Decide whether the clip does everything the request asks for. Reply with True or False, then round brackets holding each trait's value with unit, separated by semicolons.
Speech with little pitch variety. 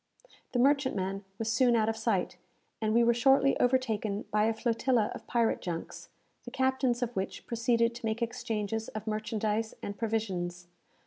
True (2.2 semitones)